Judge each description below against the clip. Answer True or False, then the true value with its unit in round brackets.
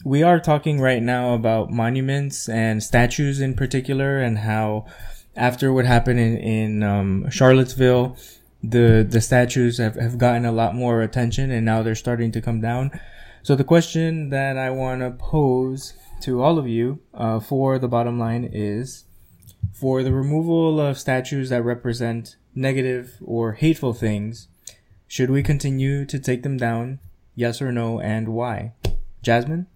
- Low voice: True (120 Hz)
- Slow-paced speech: False (160 wpm)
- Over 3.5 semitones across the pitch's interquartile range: False (2.9 semitones)